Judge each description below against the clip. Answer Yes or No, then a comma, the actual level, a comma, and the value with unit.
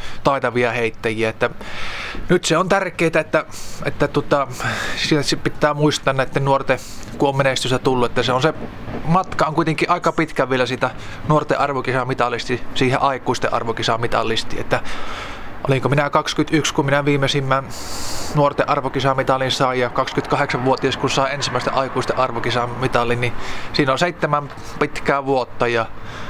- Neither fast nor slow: Yes, average, 130 wpm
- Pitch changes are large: No, average, 3.4 semitones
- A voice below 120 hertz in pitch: No, low, 135 Hz